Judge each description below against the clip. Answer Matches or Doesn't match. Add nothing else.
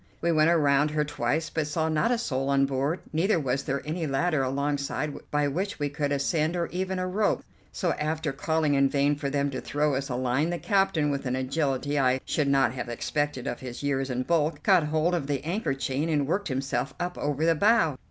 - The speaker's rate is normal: Doesn't match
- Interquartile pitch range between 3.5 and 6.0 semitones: Doesn't match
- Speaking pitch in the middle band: Matches